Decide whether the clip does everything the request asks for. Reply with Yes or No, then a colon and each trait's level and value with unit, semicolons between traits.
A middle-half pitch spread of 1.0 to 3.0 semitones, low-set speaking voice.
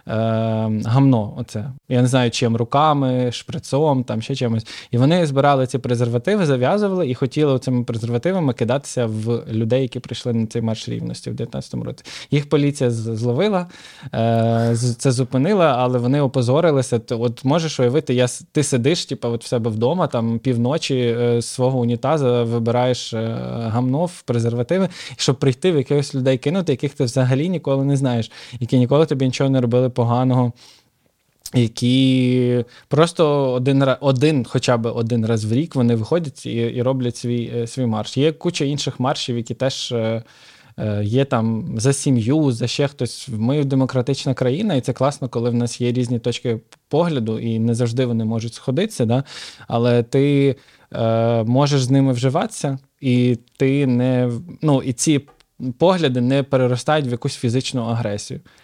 Yes: average, 2.7 semitones; low, 125 Hz